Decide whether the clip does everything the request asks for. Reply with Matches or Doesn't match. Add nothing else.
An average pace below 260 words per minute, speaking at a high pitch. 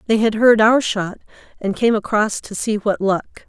Matches